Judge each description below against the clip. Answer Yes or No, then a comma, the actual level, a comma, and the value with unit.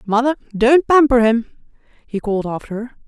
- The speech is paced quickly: No, average, 155 wpm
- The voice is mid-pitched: No, high, 240 Hz